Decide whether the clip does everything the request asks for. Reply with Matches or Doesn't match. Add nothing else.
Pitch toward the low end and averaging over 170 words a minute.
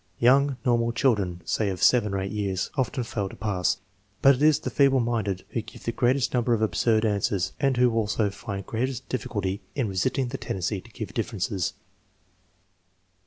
Matches